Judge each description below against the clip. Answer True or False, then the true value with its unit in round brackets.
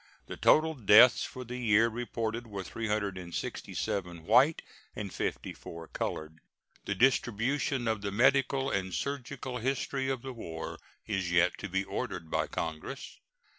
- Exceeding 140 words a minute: False (135 wpm)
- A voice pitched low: True (115 Hz)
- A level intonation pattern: False (5.2 semitones)